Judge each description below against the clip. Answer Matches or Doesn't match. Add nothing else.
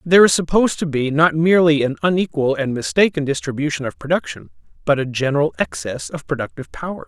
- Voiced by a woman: Doesn't match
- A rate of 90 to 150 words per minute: Doesn't match